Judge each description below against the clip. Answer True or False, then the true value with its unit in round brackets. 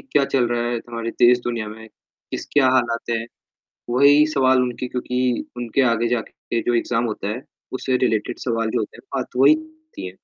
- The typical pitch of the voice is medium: False (120 Hz)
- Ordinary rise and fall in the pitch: False (2.0 semitones)